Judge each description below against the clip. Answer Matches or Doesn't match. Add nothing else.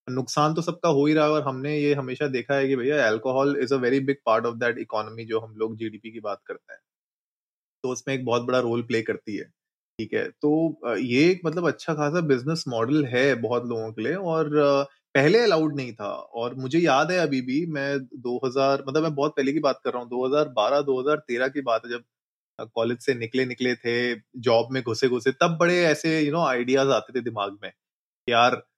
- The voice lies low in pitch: Matches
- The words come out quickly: Matches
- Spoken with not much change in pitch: Doesn't match